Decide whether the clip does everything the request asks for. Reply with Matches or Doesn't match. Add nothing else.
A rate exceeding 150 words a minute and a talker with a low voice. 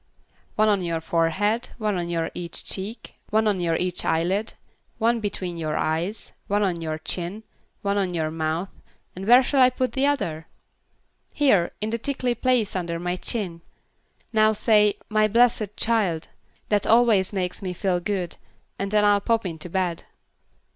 Doesn't match